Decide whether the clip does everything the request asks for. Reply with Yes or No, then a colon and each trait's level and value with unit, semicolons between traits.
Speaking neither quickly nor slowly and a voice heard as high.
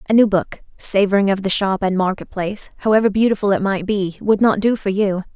No: fast, 225 wpm; high, 200 Hz